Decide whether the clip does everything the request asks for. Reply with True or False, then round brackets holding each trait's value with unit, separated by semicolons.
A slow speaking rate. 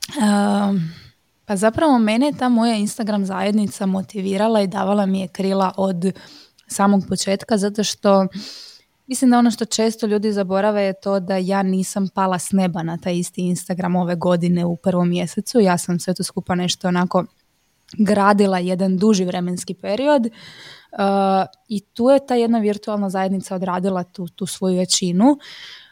False (160 wpm)